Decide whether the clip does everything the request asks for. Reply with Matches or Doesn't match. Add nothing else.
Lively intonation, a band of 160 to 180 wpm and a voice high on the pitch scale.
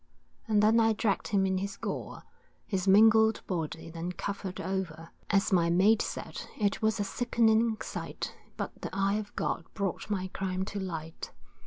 Doesn't match